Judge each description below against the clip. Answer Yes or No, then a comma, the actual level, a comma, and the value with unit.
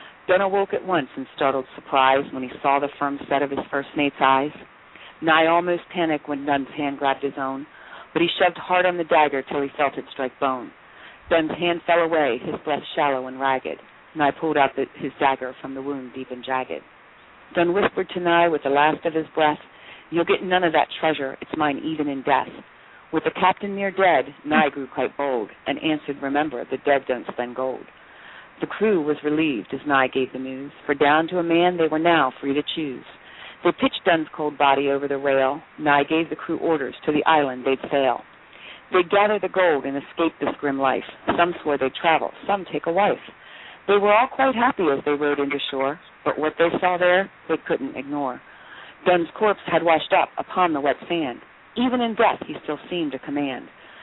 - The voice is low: No, medium, 150 Hz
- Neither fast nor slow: No, fast, 210 wpm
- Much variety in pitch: No, average, 3.7 semitones